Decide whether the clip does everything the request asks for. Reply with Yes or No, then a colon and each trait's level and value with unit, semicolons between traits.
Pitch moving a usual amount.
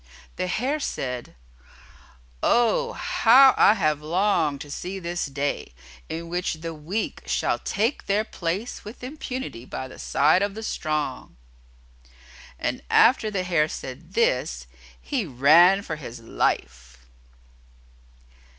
No: wide, 7.0 semitones